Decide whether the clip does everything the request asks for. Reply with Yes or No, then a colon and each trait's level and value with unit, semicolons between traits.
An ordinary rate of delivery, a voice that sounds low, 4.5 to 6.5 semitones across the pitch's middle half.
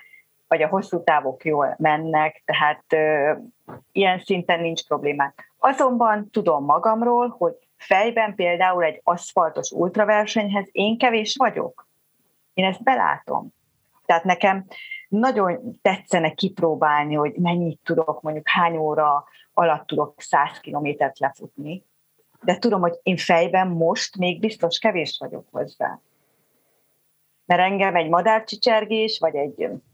No: average, 120 wpm; medium, 180 Hz; wide, 5.5 semitones